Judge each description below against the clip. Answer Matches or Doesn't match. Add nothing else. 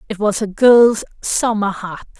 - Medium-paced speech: Matches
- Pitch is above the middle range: Matches